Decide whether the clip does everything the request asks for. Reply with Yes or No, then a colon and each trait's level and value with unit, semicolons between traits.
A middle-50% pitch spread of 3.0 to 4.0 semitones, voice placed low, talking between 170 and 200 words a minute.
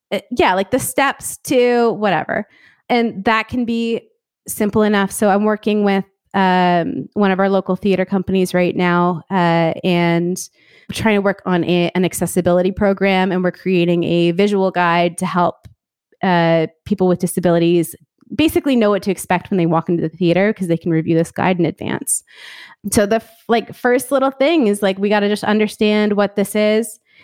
No: average, 3.3 semitones; high, 195 Hz; average, 185 wpm